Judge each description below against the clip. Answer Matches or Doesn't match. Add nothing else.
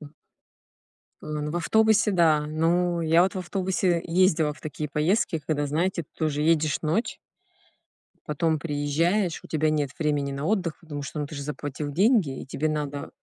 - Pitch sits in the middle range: Matches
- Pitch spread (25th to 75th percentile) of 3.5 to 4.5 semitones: Doesn't match